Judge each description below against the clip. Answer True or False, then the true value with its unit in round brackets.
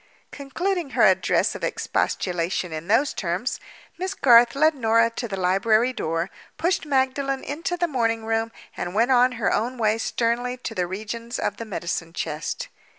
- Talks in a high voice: True (230 Hz)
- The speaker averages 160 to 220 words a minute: True (165 wpm)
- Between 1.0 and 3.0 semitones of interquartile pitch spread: False (4.6 semitones)